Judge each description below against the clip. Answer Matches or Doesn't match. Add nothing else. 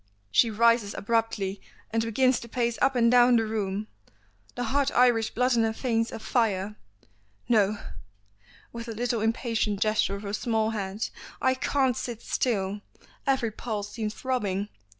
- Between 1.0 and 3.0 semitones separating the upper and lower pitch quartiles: Matches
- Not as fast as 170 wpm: Matches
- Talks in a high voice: Matches